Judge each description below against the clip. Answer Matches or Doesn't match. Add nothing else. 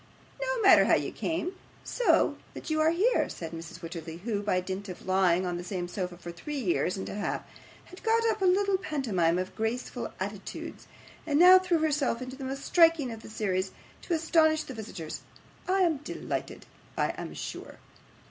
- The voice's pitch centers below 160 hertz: Doesn't match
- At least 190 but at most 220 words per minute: Matches